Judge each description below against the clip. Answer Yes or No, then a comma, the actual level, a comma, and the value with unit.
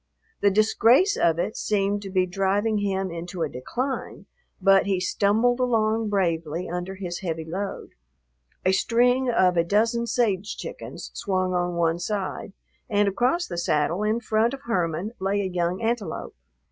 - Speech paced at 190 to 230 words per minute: No, average, 160 wpm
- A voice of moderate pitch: No, high, 195 Hz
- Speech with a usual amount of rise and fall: Yes, average, 3.8 semitones